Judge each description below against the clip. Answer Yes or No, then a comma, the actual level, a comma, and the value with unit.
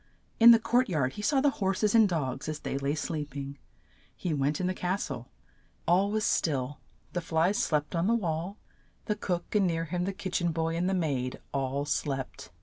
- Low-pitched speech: No, medium, 170 Hz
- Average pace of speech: No, fast, 215 wpm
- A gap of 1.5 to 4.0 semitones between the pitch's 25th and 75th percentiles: No, average, 5.2 semitones